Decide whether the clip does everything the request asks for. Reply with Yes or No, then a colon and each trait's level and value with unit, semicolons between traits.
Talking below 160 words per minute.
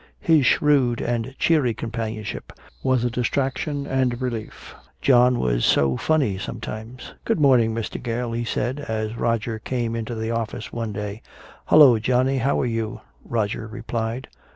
Yes: average, 150 wpm